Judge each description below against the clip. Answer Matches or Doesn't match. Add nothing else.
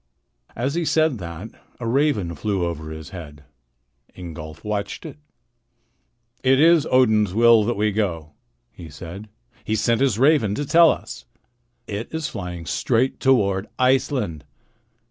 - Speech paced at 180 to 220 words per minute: Doesn't match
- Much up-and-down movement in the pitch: Matches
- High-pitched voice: Doesn't match